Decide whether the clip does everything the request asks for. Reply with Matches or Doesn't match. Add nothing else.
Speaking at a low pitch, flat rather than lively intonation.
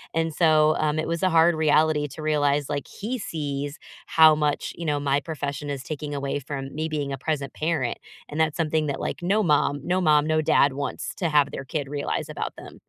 Doesn't match